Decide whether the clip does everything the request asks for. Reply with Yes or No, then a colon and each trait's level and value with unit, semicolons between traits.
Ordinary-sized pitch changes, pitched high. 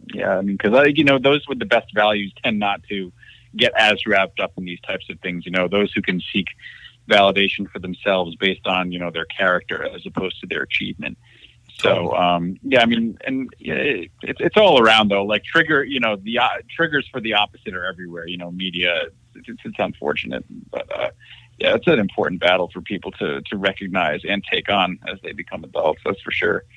No: average, 3.5 semitones; low, 100 Hz